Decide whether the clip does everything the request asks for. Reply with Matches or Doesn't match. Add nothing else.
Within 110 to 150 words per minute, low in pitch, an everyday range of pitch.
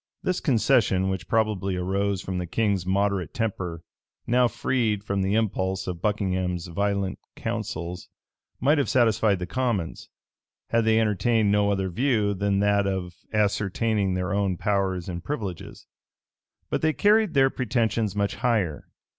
Matches